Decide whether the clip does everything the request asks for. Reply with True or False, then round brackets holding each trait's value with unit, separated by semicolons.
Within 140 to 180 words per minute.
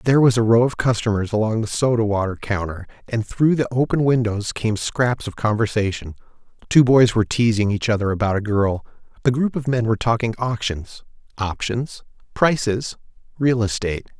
True (170 wpm)